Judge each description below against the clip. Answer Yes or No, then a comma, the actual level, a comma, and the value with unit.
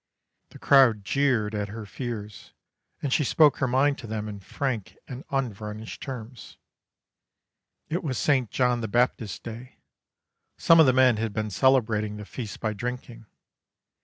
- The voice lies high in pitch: No, low, 120 Hz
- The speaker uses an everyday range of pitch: Yes, average, 3.6 semitones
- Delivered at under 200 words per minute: Yes, average, 155 wpm